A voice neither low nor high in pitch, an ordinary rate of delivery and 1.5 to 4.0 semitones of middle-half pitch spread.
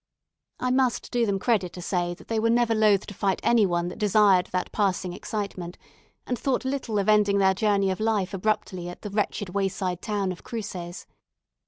No: high, 200 Hz; average, 195 wpm; average, 3.0 semitones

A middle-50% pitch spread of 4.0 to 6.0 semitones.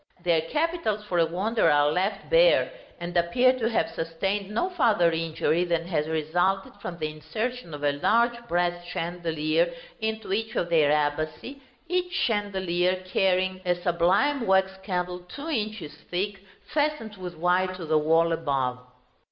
Yes: average, 4.8 semitones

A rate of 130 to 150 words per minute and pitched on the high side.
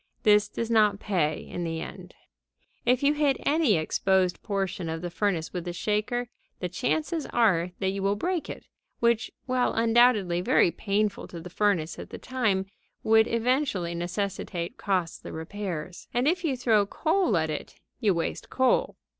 No: average, 165 wpm; high, 205 Hz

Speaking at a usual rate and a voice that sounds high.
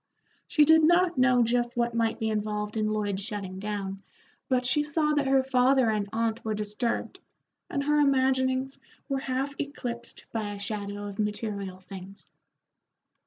Yes: average, 160 wpm; high, 235 Hz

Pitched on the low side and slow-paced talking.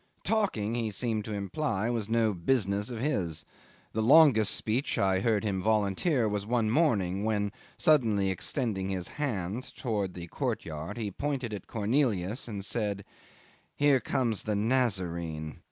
No: low, 110 Hz; average, 145 wpm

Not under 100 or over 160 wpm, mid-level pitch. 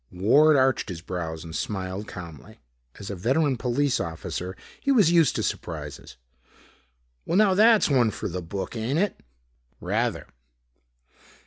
No: average, 140 wpm; low, 110 Hz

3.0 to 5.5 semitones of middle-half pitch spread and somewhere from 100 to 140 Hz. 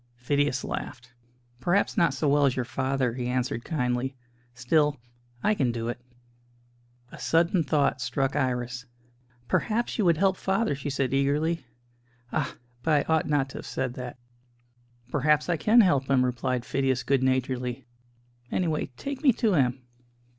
Yes: average, 4.0 semitones; low, 135 Hz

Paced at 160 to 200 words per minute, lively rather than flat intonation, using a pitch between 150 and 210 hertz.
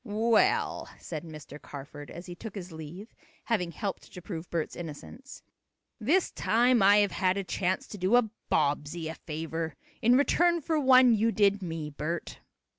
Yes: average, 170 wpm; wide, 5.9 semitones; high, 190 Hz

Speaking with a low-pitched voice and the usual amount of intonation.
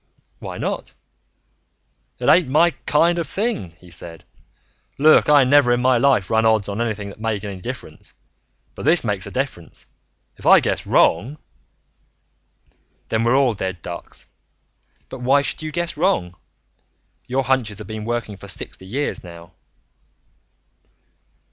No: low, 120 Hz; wide, 5.9 semitones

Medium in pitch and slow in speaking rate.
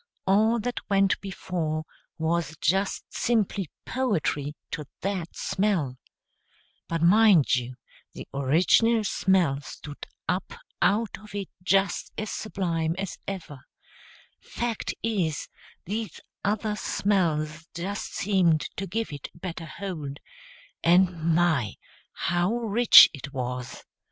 Yes: medium, 180 Hz; slow, 115 wpm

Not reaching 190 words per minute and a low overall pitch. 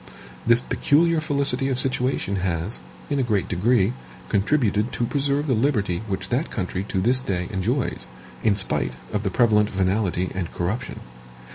Yes: average, 155 wpm; low, 110 Hz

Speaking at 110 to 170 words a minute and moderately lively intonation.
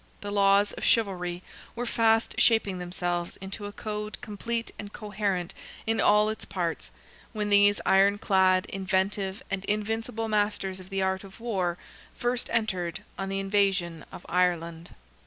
No: average, 150 wpm; narrow, 2.2 semitones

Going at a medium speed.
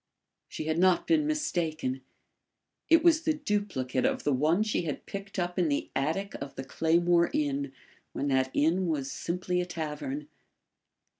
Yes: average, 160 wpm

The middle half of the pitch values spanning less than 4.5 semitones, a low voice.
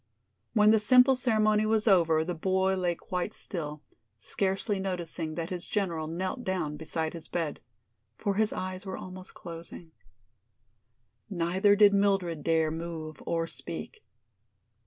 No: average, 3.5 semitones; medium, 185 Hz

